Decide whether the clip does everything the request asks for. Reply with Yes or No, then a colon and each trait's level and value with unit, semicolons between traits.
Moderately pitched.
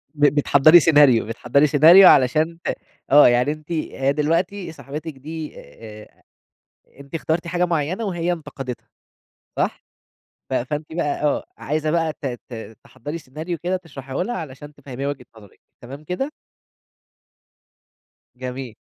Yes: medium, 150 Hz